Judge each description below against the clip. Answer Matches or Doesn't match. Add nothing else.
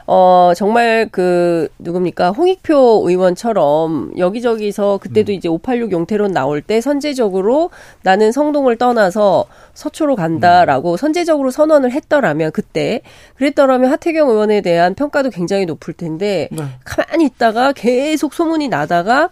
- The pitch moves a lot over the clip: Matches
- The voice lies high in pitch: Matches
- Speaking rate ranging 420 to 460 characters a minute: Doesn't match